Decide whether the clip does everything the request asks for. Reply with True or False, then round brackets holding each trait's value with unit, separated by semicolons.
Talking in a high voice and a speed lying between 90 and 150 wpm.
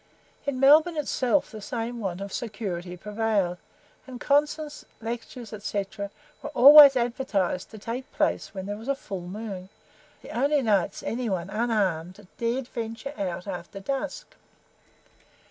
True (225 Hz; 140 wpm)